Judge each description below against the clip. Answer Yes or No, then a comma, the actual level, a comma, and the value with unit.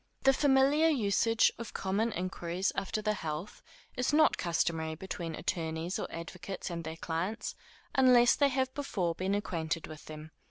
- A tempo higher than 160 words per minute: No, average, 155 wpm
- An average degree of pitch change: No, wide, 6.4 semitones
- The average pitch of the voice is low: No, high, 190 Hz